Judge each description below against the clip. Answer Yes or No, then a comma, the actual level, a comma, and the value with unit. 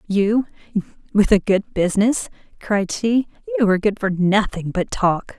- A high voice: Yes, high, 205 Hz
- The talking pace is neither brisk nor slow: Yes, average, 155 wpm